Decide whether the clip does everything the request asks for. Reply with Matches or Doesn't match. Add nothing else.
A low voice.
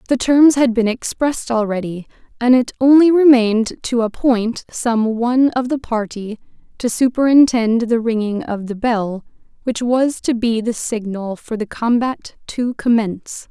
Doesn't match